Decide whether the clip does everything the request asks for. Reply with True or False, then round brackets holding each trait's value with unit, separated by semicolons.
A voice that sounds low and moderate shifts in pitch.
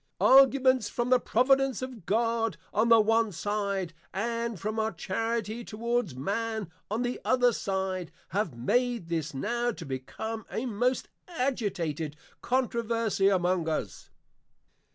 False (220 Hz; 4.2 semitones)